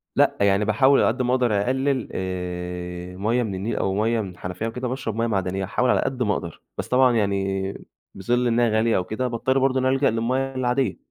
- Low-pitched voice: Yes, low, 115 Hz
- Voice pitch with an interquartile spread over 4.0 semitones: Yes, average, 4.7 semitones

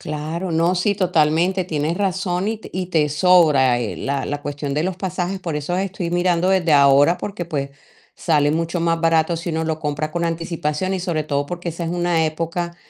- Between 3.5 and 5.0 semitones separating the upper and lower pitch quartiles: No, average, 2.9 semitones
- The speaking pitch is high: No, medium, 165 Hz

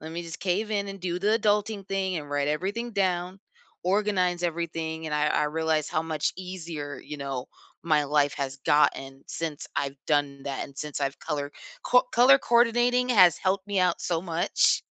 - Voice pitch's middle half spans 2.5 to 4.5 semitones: No, average, 4.9 semitones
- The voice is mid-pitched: Yes, medium, 170 Hz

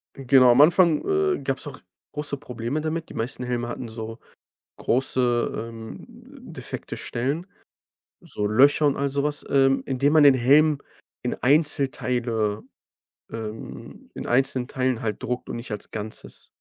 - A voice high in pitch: No, low, 130 Hz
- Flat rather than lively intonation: No, average, 3.4 semitones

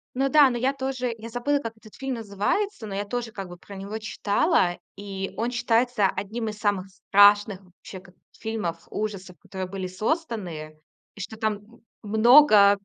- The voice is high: Yes, high, 210 Hz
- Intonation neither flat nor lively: Yes, average, 3.7 semitones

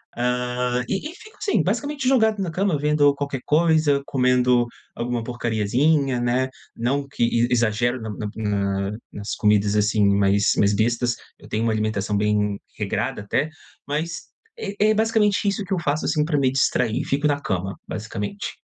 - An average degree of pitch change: No, wide, 5.8 semitones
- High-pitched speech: No, low, 125 Hz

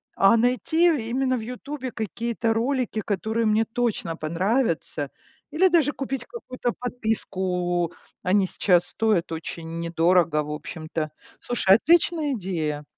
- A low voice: No, high, 220 Hz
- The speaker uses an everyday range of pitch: No, wide, 6.5 semitones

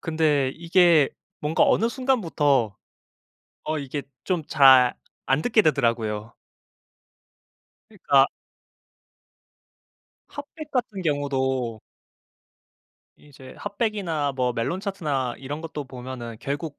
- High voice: No, medium, 145 Hz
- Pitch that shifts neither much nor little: Yes, average, 4.7 semitones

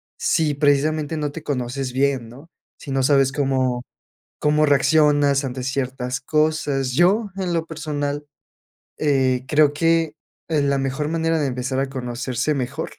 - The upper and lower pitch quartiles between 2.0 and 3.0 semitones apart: Yes, narrow, 2.6 semitones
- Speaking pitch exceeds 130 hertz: Yes, medium, 140 Hz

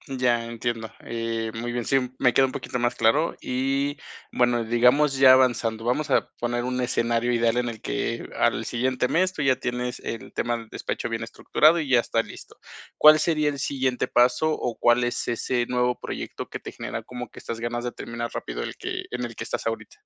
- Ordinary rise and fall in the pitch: No, narrow, 1.9 semitones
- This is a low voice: Yes, low, 120 Hz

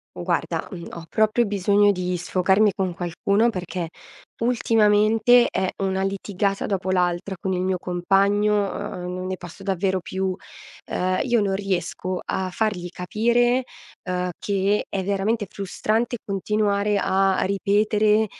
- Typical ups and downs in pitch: No, narrow, 2.2 semitones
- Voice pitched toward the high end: Yes, high, 195 Hz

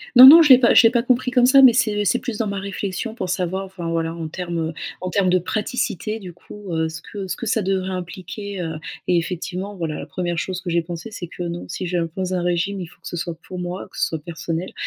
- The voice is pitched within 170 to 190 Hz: Yes, medium, 185 Hz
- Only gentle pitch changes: No, average, 3.3 semitones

